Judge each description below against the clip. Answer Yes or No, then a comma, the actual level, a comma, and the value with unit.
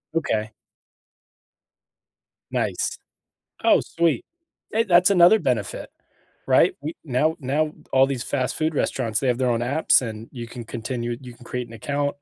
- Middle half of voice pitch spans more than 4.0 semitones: Yes, average, 4.7 semitones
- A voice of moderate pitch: No, low, 130 Hz